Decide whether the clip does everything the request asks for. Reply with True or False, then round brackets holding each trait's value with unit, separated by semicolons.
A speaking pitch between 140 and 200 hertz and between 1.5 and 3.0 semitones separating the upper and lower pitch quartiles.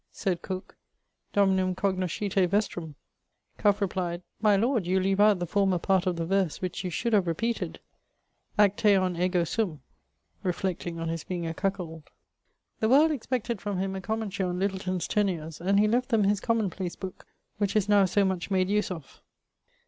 True (190 Hz; 2.5 semitones)